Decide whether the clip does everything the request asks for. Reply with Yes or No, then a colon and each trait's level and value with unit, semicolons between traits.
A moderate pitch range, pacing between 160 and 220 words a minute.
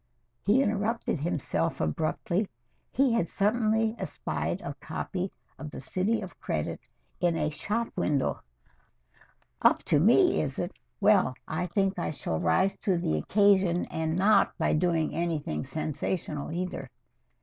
No: average, 4.9 semitones; average, 140 wpm